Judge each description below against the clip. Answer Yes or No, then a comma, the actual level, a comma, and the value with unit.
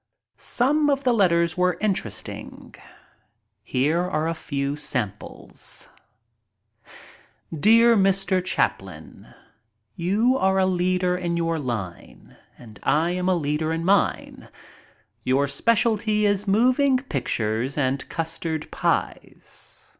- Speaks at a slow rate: Yes, slow, 115 wpm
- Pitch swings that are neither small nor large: No, wide, 5.7 semitones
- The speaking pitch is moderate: Yes, medium, 175 Hz